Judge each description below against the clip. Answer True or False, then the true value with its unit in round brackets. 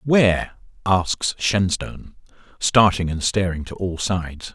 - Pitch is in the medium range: False (95 Hz)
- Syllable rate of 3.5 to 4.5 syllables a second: True (4.0 syllables/s)